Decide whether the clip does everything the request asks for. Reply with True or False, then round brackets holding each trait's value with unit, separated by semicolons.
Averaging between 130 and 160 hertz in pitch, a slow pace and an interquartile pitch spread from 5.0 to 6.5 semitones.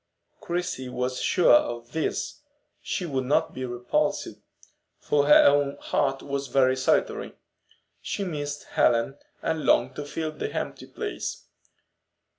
False (140 Hz; 130 wpm; 2.7 semitones)